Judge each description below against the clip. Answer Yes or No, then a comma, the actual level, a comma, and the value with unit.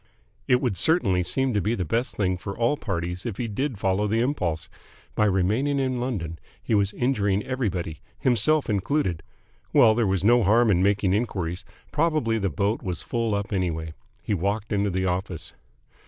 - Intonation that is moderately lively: Yes, average, 4.5 semitones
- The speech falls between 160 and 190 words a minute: Yes, average, 180 wpm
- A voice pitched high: No, low, 105 Hz